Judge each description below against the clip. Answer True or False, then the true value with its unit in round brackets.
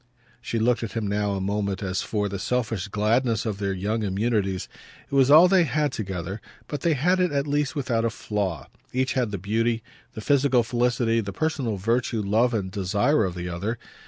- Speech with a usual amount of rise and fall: True (4.2 semitones)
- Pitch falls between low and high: False (110 Hz)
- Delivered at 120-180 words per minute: False (200 wpm)